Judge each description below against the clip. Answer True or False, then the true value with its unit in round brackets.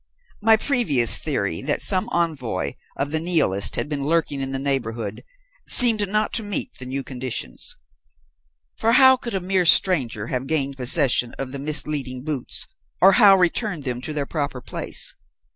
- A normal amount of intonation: False (6.5 semitones)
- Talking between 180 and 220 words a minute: False (165 wpm)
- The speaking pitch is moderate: True (145 Hz)